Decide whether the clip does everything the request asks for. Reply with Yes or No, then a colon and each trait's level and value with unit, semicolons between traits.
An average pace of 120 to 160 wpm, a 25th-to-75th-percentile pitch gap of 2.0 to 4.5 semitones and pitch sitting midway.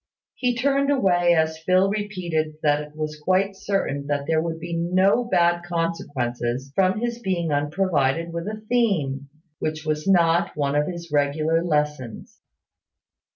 Yes: average, 150 wpm; average, 4.1 semitones; medium, 165 Hz